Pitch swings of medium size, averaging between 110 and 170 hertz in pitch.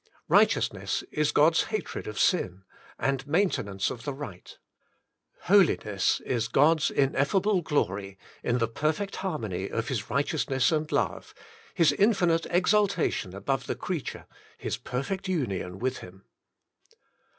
No: wide, 7.5 semitones; medium, 140 Hz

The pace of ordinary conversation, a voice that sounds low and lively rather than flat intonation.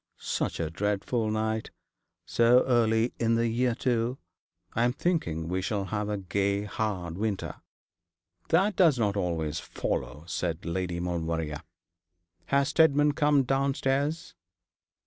No: slow, 125 wpm; low, 110 Hz; wide, 6.4 semitones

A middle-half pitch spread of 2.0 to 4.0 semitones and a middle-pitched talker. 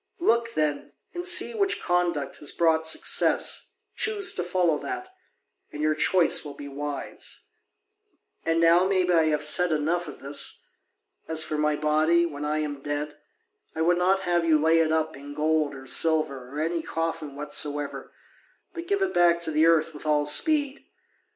Yes: average, 2.9 semitones; medium, 160 Hz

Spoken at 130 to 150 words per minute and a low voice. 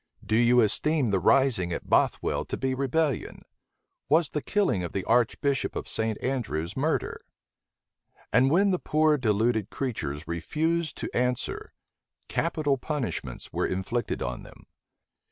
Yes: slow, 135 wpm; low, 125 Hz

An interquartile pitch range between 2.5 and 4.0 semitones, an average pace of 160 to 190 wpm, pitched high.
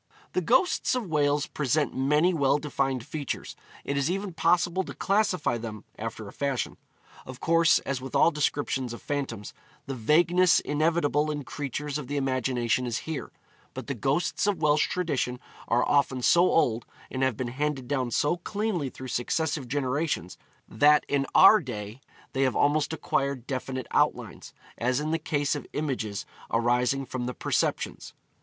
No: average, 3.6 semitones; average, 165 wpm; medium, 140 Hz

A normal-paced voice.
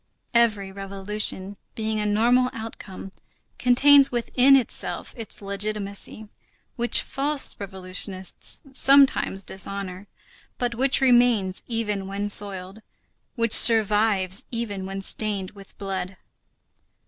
No: slow, 100 wpm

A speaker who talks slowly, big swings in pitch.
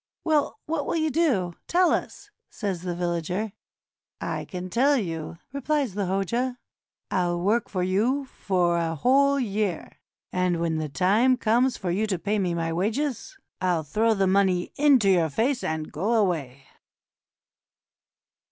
No: average, 150 wpm; wide, 6.3 semitones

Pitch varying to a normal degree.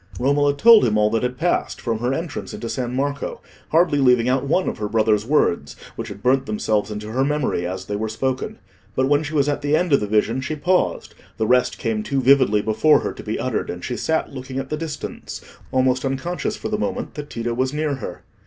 Yes: average, 4.6 semitones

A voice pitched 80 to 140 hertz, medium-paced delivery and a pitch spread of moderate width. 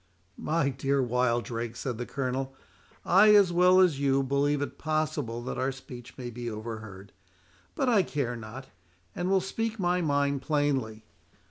Yes: low, 135 Hz; average, 155 wpm; average, 4.8 semitones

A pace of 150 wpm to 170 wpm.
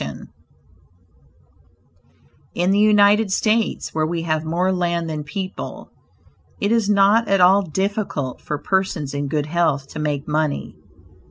No: average, 140 wpm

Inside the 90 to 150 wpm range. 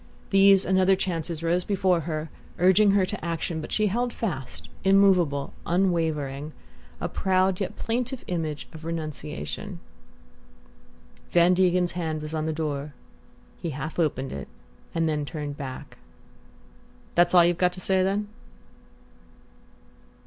Yes: slow, 135 wpm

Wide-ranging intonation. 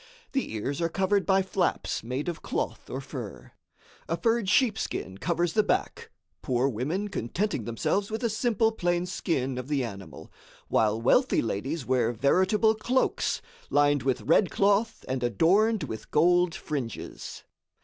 Yes: wide, 8.3 semitones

